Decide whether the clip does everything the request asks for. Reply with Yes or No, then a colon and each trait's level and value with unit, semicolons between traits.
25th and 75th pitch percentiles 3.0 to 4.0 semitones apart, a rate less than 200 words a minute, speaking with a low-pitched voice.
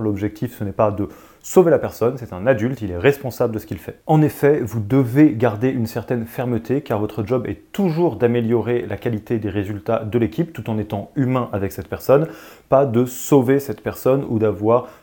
No: average, 3.5 semitones; average, 210 wpm; low, 120 Hz